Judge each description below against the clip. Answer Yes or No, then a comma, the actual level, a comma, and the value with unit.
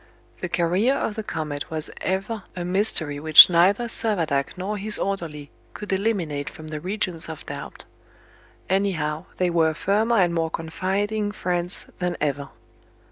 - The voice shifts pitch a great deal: No, average, 4.2 semitones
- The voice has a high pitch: No, medium, 180 Hz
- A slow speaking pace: No, average, 145 wpm